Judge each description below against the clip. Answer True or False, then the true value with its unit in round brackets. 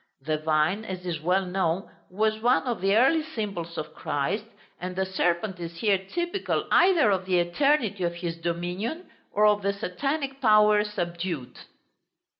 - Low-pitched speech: False (190 Hz)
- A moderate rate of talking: True (160 wpm)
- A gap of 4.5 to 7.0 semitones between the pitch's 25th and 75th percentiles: False (4.1 semitones)